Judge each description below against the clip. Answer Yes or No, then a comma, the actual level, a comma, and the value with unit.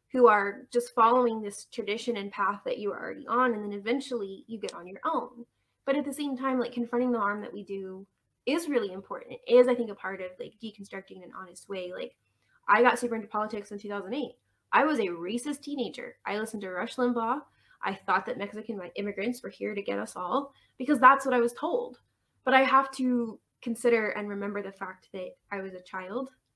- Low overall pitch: No, high, 230 Hz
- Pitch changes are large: No, average, 4.0 semitones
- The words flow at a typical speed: No, fast, 220 wpm